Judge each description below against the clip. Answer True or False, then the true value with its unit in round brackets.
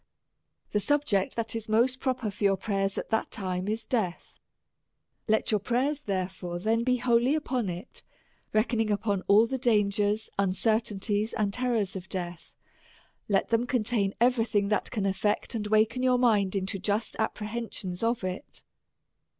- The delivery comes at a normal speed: True (160 wpm)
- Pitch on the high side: True (215 Hz)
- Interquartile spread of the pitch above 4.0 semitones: False (3.1 semitones)